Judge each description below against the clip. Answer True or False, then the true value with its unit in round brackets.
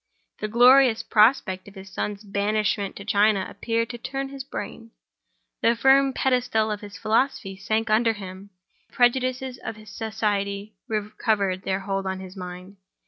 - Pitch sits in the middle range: False (215 Hz)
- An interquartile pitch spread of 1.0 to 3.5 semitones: True (3.1 semitones)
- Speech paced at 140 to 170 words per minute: True (150 wpm)